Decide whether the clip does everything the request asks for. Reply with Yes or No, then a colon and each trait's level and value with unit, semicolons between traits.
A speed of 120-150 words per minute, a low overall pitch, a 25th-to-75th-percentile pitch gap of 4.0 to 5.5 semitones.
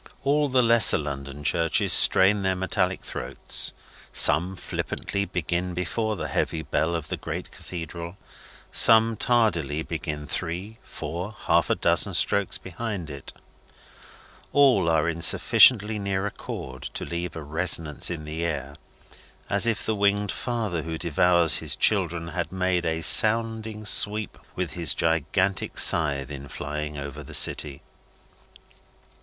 Yes: average, 140 wpm; very low, 85 Hz; average, 4.5 semitones